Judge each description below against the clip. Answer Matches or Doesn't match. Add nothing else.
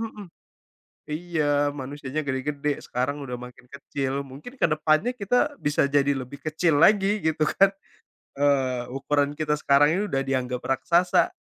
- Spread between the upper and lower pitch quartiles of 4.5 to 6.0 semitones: Doesn't match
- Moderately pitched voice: Matches